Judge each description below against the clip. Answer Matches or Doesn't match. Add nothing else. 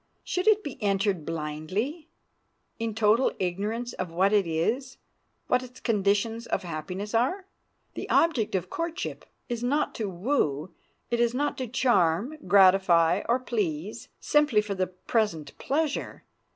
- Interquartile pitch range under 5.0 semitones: Doesn't match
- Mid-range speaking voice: Doesn't match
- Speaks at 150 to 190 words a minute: Doesn't match